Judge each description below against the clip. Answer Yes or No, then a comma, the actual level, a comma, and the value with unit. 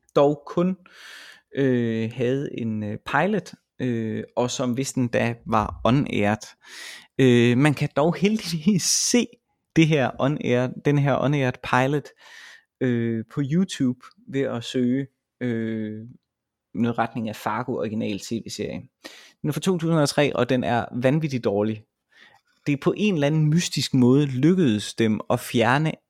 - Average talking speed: No, slow, 140 wpm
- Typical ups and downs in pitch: Yes, average, 4.3 semitones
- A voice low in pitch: Yes, low, 130 Hz